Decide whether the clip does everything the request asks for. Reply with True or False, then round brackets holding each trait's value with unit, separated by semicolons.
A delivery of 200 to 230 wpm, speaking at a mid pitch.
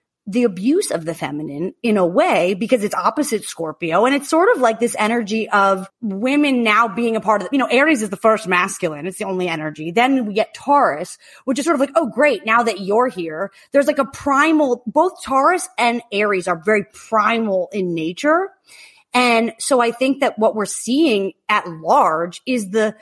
False (205 wpm; 225 Hz)